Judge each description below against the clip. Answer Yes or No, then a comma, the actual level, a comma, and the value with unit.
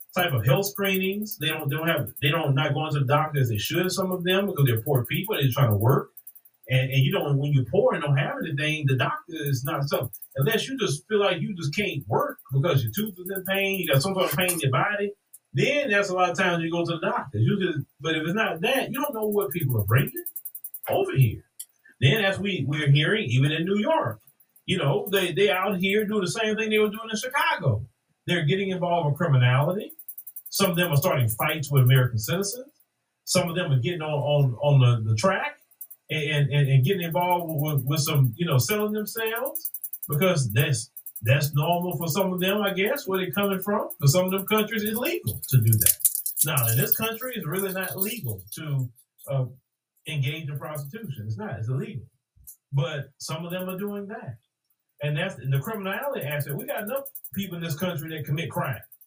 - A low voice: No, medium, 155 Hz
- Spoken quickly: Yes, fast, 225 wpm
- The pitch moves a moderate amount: No, wide, 6.2 semitones